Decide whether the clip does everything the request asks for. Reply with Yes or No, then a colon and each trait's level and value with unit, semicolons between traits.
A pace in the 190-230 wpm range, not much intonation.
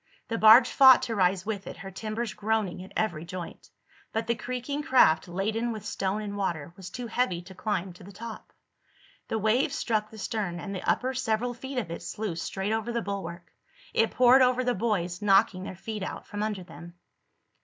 No: average, 200 wpm; average, 3.8 semitones